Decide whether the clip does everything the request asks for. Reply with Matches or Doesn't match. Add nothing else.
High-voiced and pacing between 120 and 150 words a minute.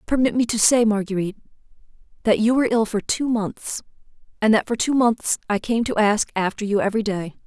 Doesn't match